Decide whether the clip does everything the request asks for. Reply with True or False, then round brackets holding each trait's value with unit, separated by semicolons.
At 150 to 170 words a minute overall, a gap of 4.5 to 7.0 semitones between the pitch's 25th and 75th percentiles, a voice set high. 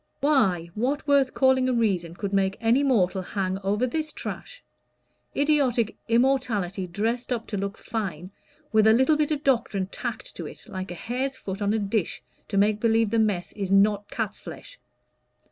False (180 wpm; 4.8 semitones; 220 Hz)